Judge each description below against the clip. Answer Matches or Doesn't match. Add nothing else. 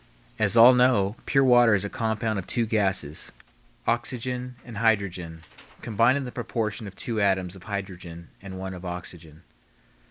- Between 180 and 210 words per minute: Doesn't match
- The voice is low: Matches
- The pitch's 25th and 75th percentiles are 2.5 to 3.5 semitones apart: Doesn't match